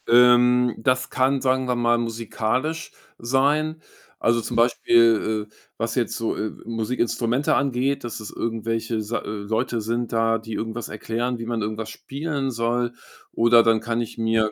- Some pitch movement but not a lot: No, narrow, 1.7 semitones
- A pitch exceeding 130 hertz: No, low, 115 Hz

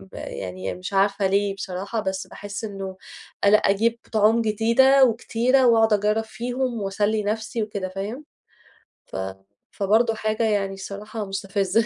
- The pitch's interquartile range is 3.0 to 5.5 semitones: No, narrow, 2.5 semitones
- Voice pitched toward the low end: No, high, 210 Hz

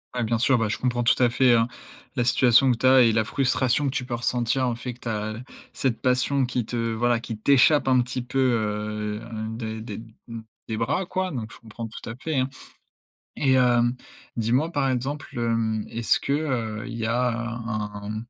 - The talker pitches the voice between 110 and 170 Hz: Yes, low, 120 Hz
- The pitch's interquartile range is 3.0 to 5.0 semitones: No, narrow, 2.5 semitones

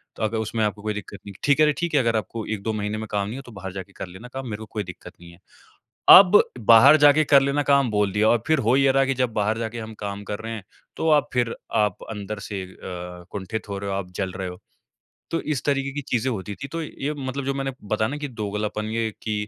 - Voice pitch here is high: No, low, 110 Hz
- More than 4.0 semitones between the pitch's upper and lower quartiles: Yes, average, 5.0 semitones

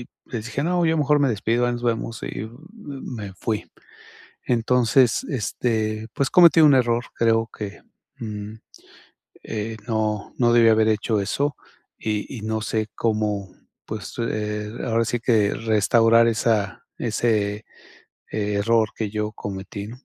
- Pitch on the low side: Yes, low, 110 Hz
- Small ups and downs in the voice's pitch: Yes, narrow, 2.0 semitones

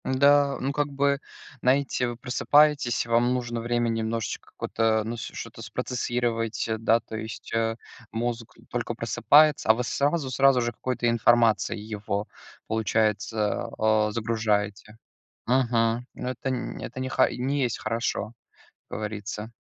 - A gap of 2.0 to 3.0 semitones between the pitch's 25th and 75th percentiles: Yes, narrow, 2.5 semitones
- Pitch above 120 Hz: No, low, 115 Hz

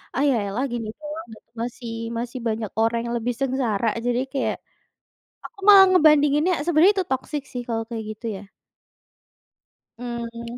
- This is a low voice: No, high, 245 Hz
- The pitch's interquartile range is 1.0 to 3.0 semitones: No, average, 4.3 semitones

